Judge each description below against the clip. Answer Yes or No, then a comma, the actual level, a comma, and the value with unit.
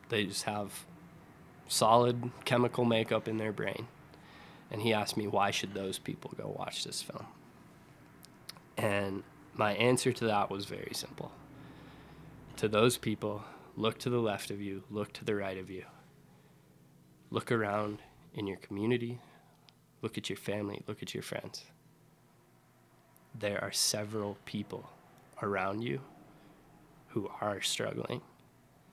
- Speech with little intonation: No, average, 3.2 semitones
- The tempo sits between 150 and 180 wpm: No, slow, 135 wpm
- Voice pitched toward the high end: No, low, 110 Hz